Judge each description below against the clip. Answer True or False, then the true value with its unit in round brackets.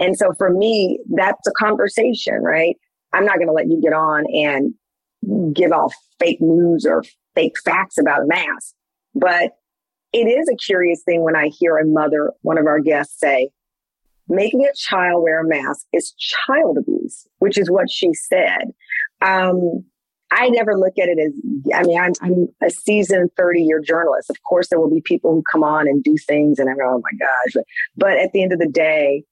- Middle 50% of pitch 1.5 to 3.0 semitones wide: False (4.2 semitones)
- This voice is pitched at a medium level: True (175 Hz)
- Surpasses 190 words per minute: True (205 wpm)